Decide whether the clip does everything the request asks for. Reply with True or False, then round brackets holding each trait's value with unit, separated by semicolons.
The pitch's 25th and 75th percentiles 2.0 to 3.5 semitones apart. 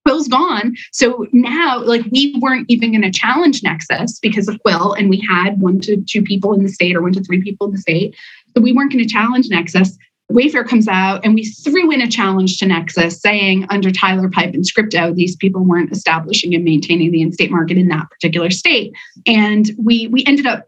False (4.6 semitones)